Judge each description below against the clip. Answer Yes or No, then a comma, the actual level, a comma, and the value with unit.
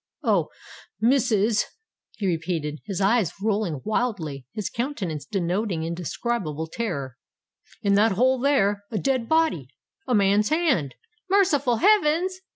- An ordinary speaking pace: No, slow, 115 wpm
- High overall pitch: Yes, high, 210 Hz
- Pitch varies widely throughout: Yes, wide, 6.7 semitones